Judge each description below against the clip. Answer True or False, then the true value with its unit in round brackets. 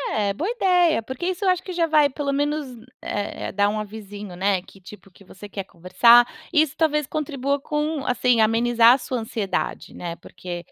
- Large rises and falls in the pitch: True (6.8 semitones)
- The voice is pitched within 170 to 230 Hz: False (240 Hz)